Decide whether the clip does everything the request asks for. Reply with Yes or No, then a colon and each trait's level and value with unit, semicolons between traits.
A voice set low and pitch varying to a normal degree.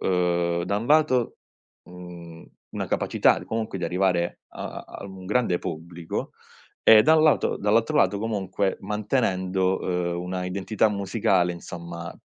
Yes: very low, 95 Hz; average, 3.2 semitones